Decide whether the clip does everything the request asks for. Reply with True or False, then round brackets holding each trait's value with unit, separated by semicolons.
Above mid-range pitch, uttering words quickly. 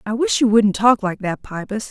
True (220 Hz; 250 wpm)